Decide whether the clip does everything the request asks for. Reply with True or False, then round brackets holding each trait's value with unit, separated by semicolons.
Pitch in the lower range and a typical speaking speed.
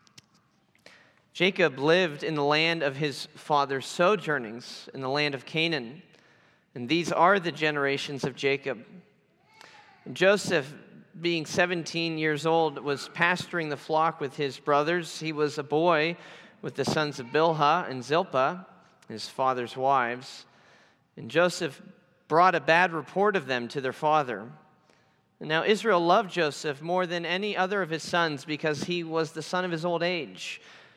False (160 Hz; 155 wpm)